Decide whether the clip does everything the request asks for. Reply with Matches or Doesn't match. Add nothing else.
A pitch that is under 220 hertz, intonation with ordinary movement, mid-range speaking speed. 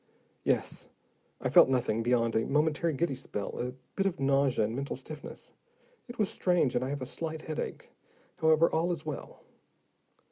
Matches